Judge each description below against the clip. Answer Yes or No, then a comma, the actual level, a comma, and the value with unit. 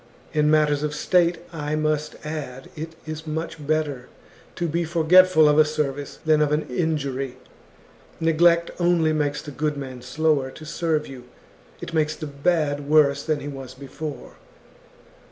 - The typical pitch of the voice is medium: Yes, medium, 150 Hz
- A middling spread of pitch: No, narrow, 1.8 semitones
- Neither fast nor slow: Yes, average, 155 wpm